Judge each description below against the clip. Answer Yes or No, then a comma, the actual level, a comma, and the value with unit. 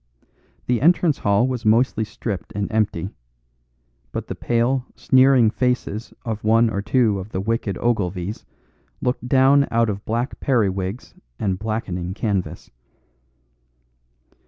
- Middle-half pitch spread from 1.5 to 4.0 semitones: Yes, average, 3.7 semitones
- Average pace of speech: No, slow, 125 wpm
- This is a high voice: No, low, 110 Hz